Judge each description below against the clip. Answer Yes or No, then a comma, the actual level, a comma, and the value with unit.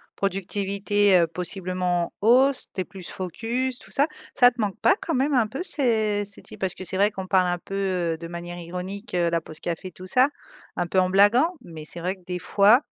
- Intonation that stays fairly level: No, average, 3.6 semitones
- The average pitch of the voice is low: No, high, 190 Hz